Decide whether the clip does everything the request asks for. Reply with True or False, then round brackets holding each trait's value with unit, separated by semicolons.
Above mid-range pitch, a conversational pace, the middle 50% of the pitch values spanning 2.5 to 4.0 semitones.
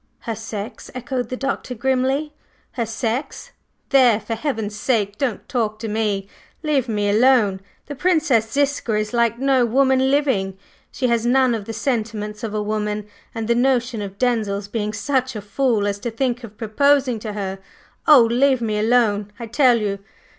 True (230 Hz; 175 wpm; 3.6 semitones)